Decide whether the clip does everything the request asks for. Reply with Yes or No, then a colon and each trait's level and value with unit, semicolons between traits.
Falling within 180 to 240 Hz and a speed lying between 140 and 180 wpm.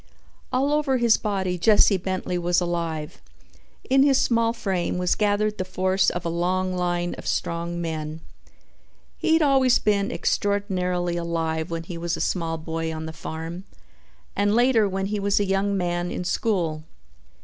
Yes: medium, 185 Hz; average, 165 wpm